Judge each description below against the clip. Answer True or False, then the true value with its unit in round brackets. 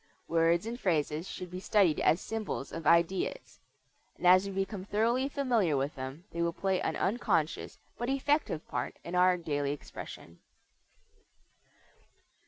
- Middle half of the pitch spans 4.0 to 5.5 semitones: True (4.4 semitones)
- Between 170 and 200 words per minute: False (145 wpm)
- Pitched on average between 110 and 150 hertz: False (180 Hz)